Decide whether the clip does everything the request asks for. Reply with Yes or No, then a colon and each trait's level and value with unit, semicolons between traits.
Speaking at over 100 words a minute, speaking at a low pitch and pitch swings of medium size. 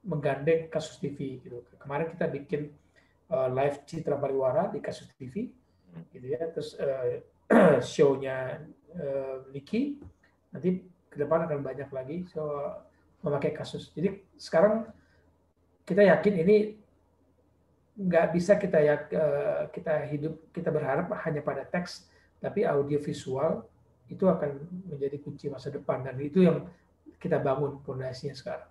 No: average, 125 wpm; medium, 150 Hz; average, 4.3 semitones